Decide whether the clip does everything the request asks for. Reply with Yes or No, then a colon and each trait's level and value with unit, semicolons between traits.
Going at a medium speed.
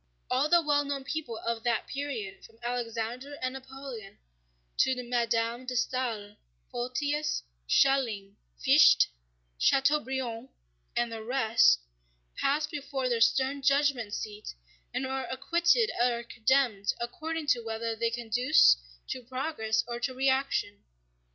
No: slow, 125 wpm